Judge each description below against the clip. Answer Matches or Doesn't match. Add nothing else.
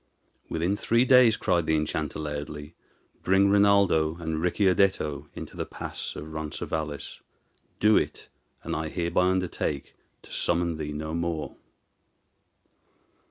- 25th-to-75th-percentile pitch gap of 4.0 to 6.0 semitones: Doesn't match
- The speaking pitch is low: Matches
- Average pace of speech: Doesn't match